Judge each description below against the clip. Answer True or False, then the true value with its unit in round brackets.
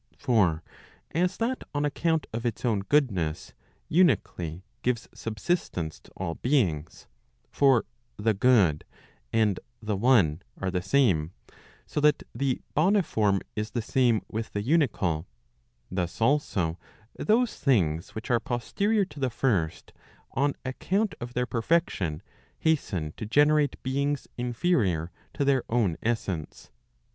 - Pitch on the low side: True (120 Hz)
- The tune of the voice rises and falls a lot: True (7.3 semitones)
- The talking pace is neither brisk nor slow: False (130 wpm)